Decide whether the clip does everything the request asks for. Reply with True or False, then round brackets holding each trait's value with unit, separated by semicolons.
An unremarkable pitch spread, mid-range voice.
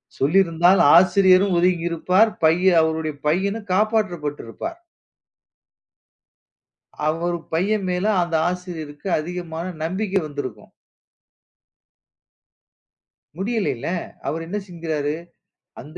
True (3.1 semitones; 175 Hz)